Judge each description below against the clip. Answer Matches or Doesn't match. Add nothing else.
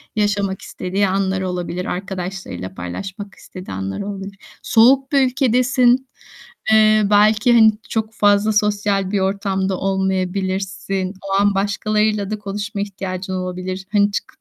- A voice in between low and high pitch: Doesn't match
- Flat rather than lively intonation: Matches